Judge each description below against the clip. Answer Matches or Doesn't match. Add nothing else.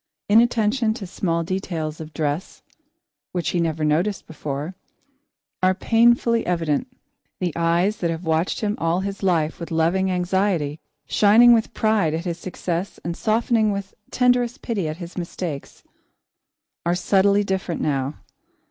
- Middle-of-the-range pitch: Matches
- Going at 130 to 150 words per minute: Matches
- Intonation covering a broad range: Doesn't match